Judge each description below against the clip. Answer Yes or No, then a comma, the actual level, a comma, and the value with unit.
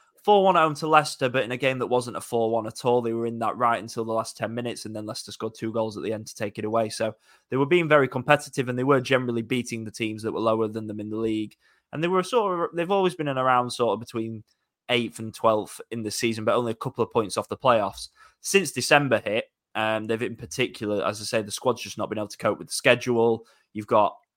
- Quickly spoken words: Yes, fast, 265 wpm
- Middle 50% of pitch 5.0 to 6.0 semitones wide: No, average, 2.9 semitones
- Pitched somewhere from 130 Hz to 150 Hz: No, low, 115 Hz